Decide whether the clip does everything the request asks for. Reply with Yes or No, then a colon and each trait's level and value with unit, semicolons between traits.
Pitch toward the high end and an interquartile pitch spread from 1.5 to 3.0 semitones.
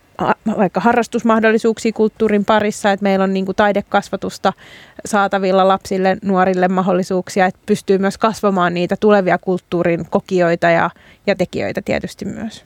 Yes: high, 195 Hz; narrow, 2.5 semitones